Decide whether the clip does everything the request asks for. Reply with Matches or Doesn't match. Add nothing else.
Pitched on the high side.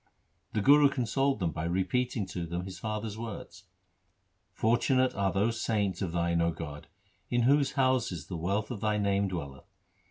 Doesn't match